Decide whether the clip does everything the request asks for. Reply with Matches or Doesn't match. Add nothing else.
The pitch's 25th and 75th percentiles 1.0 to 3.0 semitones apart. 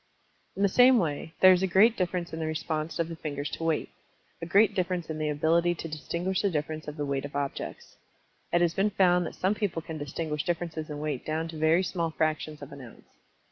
Matches